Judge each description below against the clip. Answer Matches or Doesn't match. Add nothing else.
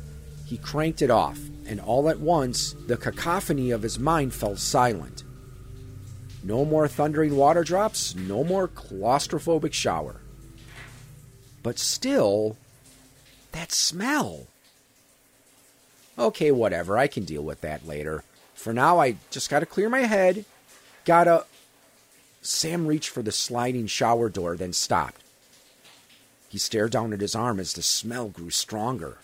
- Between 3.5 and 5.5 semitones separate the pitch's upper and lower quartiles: Matches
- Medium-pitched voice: Doesn't match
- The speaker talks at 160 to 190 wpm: Doesn't match